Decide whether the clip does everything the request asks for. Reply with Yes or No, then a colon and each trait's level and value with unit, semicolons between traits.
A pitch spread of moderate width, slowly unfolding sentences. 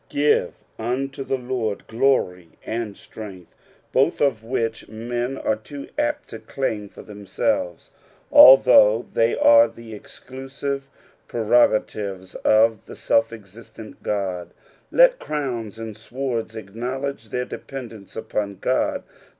Yes: average, 3.6 semitones; slow, 125 wpm